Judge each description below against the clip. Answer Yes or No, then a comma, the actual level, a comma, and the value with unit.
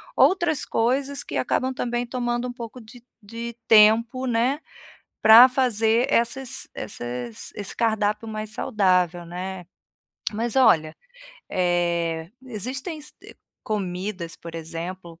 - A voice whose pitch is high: Yes, high, 220 Hz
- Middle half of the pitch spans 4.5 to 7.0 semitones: Yes, average, 5.2 semitones